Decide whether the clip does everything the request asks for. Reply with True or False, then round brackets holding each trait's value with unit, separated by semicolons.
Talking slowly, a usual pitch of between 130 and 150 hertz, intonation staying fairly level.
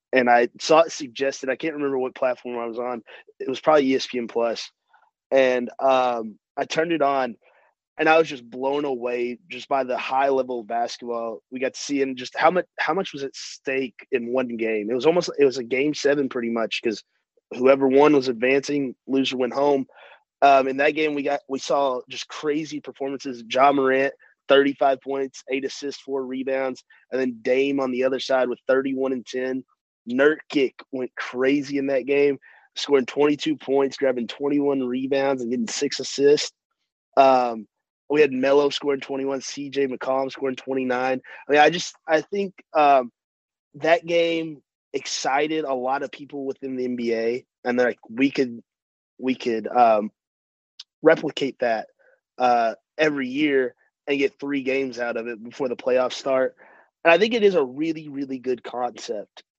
False (180 wpm; 135 Hz; 2.2 semitones)